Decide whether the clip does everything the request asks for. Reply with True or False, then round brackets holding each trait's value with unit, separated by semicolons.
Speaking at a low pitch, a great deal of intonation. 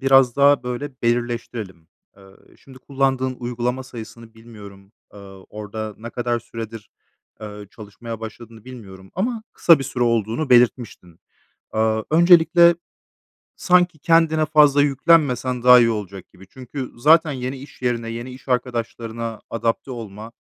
False (120 Hz; 3.4 semitones)